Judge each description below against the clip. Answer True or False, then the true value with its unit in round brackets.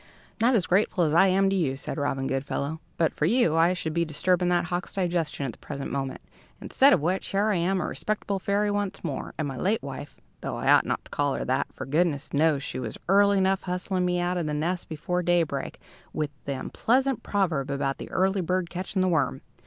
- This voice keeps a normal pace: False (225 wpm)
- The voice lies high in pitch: False (175 Hz)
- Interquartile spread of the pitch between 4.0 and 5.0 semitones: True (4.4 semitones)